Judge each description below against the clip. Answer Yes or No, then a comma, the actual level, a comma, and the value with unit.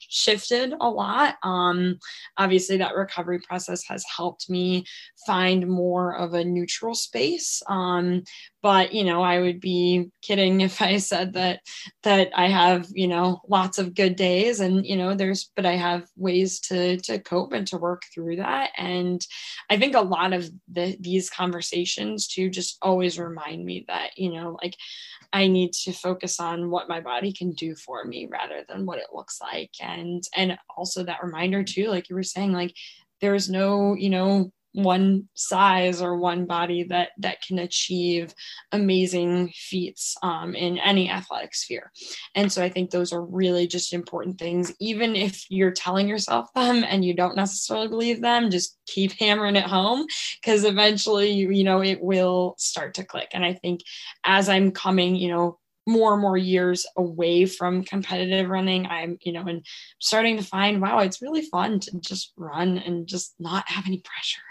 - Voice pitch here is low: No, medium, 185 Hz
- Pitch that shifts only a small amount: Yes, narrow, 1.7 semitones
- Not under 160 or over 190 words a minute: Yes, average, 180 wpm